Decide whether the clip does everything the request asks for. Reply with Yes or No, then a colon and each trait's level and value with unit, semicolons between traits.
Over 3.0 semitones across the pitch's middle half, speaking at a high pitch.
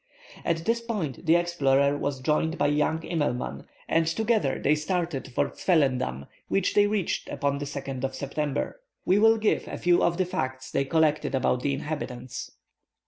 No: average, 4.3 semitones; medium, 150 Hz